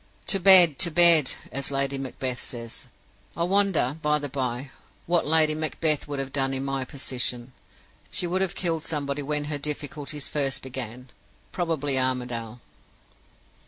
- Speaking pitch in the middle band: Yes, medium, 145 Hz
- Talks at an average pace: Yes, average, 150 wpm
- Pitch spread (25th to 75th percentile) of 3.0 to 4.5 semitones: Yes, average, 3.3 semitones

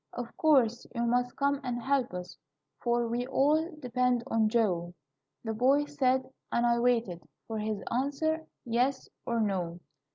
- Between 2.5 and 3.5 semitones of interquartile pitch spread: Yes, average, 2.9 semitones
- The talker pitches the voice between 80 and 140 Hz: No, high, 240 Hz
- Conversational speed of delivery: Yes, average, 155 wpm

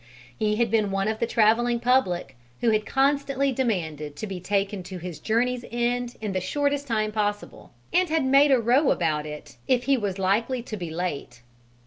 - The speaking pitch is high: Yes, high, 220 Hz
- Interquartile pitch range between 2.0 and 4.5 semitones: No, average, 5.0 semitones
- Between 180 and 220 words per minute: Yes, average, 190 wpm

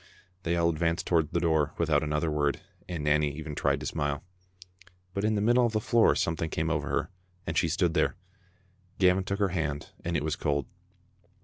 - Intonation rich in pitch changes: No, average, 3.1 semitones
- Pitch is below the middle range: Yes, very low, 80 Hz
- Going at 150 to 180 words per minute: No, fast, 205 wpm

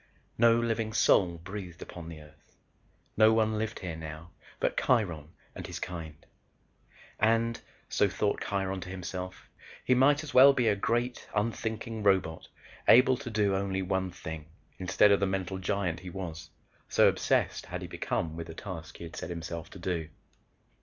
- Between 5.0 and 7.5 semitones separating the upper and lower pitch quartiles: No, average, 4.5 semitones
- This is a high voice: No, very low, 95 Hz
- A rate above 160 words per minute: Yes, average, 170 wpm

